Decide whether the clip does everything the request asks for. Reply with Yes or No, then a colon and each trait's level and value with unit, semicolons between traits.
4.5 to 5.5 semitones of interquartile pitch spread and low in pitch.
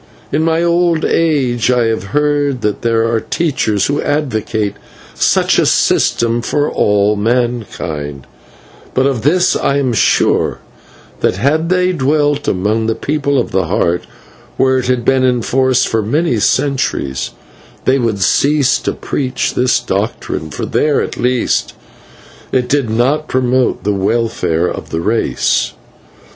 Yes: average, 4.8 semitones; low, 125 Hz